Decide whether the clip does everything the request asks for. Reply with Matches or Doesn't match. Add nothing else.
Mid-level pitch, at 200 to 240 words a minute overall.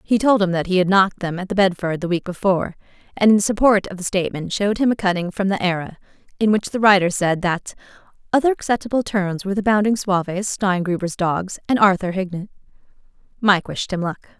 Doesn't match